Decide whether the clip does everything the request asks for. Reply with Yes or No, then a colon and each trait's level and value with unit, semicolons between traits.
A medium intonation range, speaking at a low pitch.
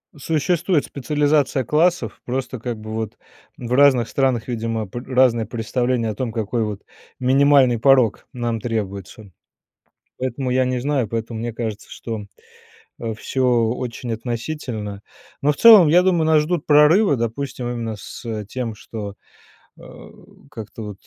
Yes: average, 3.9 semitones; low, 120 Hz